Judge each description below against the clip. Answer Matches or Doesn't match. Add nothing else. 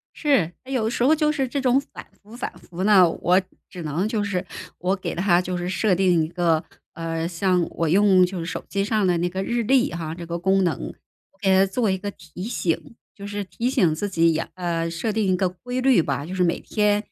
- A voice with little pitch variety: Doesn't match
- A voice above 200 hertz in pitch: Doesn't match